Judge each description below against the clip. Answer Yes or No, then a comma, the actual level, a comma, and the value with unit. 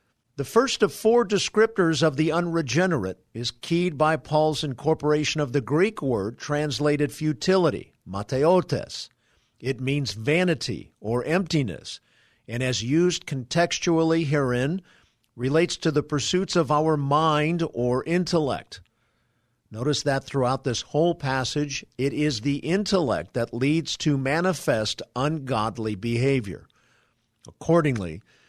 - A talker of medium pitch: Yes, medium, 145 Hz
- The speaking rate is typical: No, slow, 120 wpm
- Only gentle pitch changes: No, average, 4.8 semitones